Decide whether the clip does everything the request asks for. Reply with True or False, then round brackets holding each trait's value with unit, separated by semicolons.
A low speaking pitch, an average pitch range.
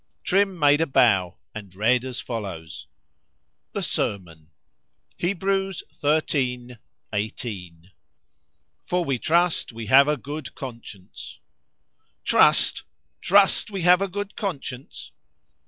False (130 Hz; 8.6 semitones)